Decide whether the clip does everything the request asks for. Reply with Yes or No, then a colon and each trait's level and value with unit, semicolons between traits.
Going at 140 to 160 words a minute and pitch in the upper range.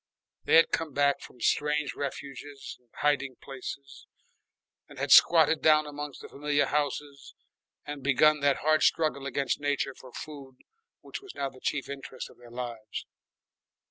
No: average, 155 wpm; medium, 140 Hz